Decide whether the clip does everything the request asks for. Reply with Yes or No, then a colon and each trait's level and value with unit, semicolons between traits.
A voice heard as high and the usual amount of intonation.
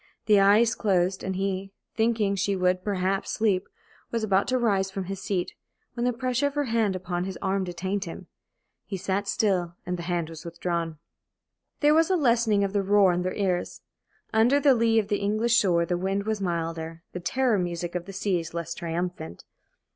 Yes: high, 195 Hz; average, 3.5 semitones